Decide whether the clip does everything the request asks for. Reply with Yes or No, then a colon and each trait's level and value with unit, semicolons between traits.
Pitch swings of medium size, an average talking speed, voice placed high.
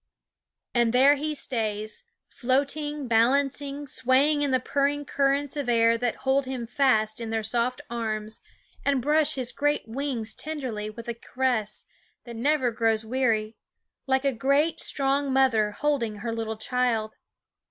Yes: average, 3.8 semitones; average, 150 wpm; very high, 255 Hz